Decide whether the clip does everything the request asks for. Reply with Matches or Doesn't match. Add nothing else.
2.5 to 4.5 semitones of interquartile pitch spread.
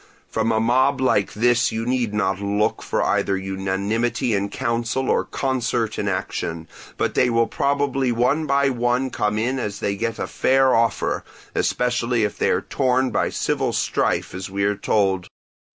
Matches